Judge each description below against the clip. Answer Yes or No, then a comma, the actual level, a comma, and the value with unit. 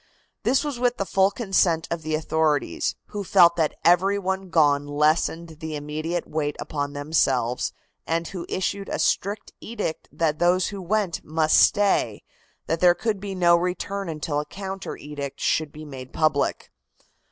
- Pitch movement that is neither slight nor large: Yes, average, 4.1 semitones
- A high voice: No, medium, 165 Hz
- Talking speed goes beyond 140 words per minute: Yes, average, 165 wpm